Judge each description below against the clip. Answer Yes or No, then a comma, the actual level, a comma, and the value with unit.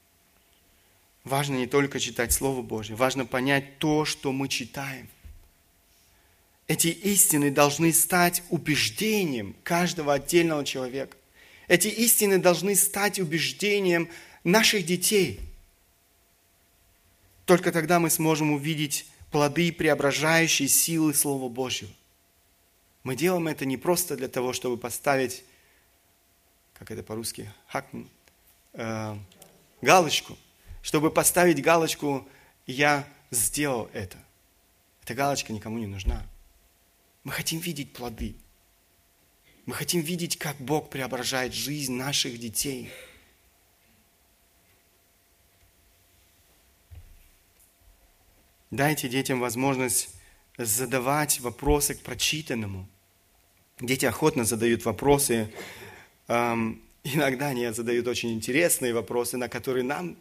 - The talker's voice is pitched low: Yes, low, 125 Hz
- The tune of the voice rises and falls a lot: Yes, wide, 7.5 semitones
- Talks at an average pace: No, slow, 95 wpm